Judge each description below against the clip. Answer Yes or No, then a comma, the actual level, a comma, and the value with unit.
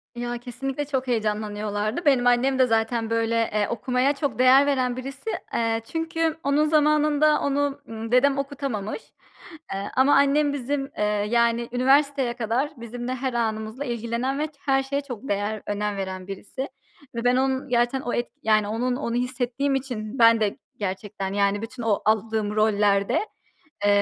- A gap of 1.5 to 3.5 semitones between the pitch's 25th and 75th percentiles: No, average, 3.9 semitones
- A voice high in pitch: Yes, high, 245 Hz